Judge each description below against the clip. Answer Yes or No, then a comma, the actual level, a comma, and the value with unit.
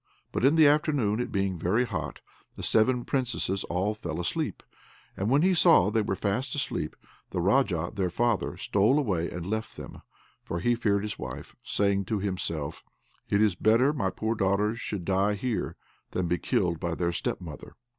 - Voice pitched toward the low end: Yes, low, 100 Hz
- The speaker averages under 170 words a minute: No, average, 185 wpm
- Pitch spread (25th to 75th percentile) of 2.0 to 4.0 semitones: No, average, 4.8 semitones